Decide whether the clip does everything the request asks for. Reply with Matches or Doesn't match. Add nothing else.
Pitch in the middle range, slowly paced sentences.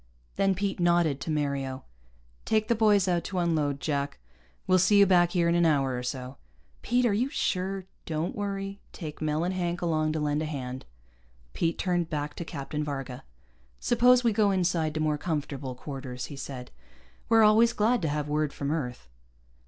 Doesn't match